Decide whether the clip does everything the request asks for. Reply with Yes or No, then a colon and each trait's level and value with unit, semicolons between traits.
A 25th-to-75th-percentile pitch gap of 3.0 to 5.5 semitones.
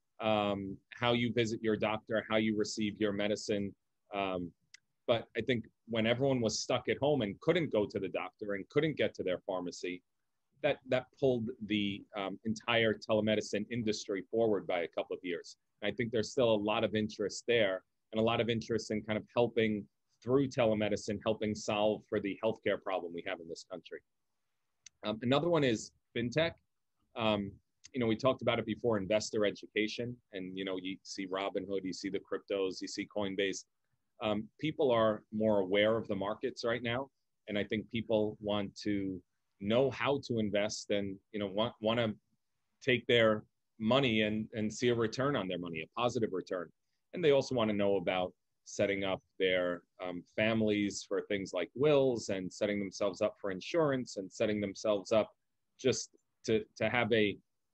No: narrow, 2.4 semitones